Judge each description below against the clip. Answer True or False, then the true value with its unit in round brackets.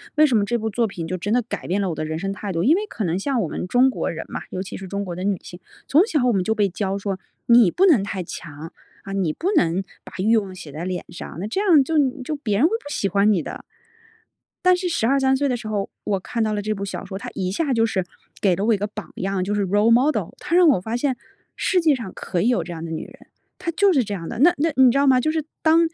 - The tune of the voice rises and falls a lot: True (6.3 semitones)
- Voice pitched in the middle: False (210 Hz)